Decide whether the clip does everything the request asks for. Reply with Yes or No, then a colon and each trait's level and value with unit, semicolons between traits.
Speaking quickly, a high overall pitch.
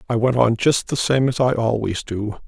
No: fast, 245 wpm; low, 120 Hz